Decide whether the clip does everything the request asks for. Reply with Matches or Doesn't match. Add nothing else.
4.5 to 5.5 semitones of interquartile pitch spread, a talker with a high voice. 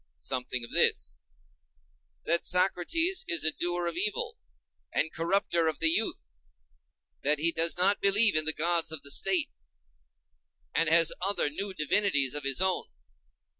Doesn't match